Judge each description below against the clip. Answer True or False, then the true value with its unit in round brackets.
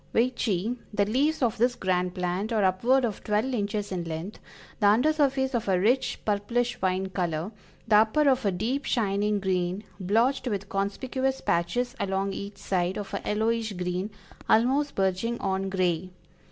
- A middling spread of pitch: True (4.4 semitones)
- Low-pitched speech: False (205 Hz)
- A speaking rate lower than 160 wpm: False (165 wpm)